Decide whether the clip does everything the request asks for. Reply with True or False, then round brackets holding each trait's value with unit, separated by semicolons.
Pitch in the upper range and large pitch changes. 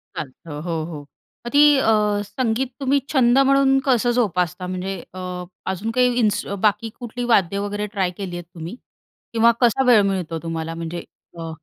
True (205 Hz; 5.9 semitones)